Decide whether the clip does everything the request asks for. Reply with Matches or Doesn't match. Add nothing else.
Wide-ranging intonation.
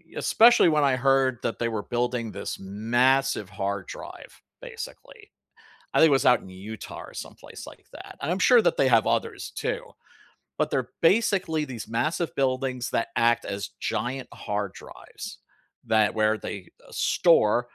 Doesn't match